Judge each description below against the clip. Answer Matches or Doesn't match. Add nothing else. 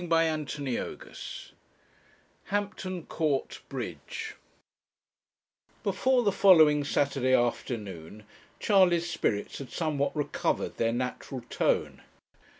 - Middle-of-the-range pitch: Matches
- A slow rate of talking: Matches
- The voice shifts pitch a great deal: Matches